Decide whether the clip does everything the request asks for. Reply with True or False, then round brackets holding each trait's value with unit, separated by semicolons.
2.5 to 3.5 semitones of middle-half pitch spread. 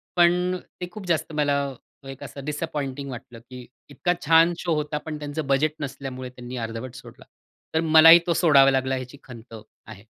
False (3.9 semitones)